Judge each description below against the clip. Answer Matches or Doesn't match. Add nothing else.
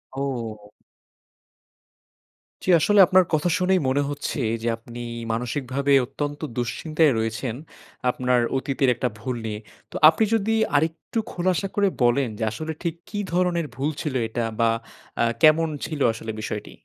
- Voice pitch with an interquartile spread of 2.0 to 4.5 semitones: Doesn't match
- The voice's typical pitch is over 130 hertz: Matches